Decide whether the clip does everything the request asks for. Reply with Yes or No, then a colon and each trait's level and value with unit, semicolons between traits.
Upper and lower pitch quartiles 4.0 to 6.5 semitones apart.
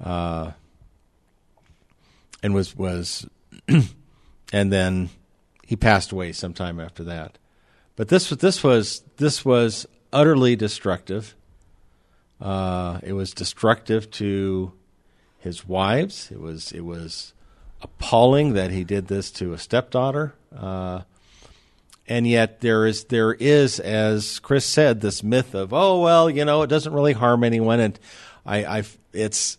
Yes: average, 5.2 semitones